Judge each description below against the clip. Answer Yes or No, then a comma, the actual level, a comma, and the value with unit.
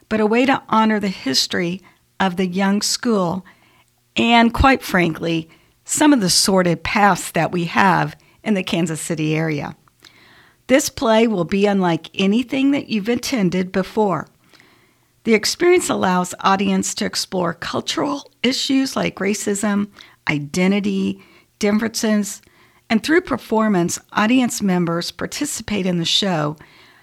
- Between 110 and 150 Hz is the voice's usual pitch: No, high, 200 Hz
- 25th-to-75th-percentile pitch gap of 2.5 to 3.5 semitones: No, average, 4.3 semitones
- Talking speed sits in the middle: No, slow, 130 wpm